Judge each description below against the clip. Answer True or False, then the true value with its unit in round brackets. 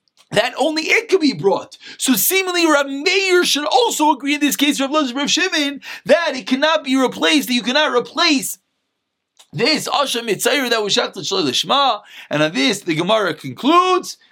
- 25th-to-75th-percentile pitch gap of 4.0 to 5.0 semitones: True (4.7 semitones)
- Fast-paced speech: False (165 wpm)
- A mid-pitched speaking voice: False (285 Hz)